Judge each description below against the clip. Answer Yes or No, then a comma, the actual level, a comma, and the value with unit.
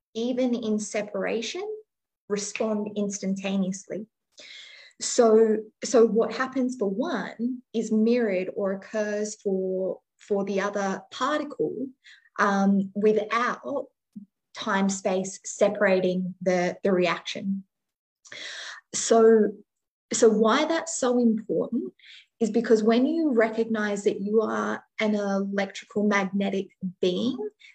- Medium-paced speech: No, slow, 100 wpm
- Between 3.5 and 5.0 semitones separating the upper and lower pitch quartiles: No, average, 2.7 semitones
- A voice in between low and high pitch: No, high, 210 Hz